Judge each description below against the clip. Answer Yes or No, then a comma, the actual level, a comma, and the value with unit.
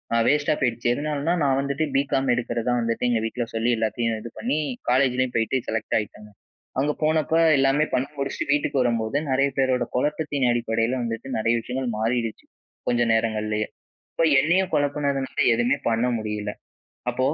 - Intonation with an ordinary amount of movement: Yes, average, 3.4 semitones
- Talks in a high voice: No, low, 125 Hz